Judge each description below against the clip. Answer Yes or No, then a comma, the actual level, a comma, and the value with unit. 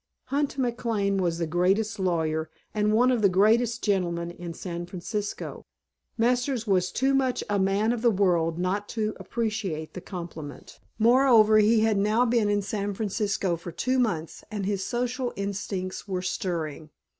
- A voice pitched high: Yes, high, 205 Hz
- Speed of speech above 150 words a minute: Yes, average, 160 wpm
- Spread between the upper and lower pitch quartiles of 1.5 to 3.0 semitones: No, average, 4.0 semitones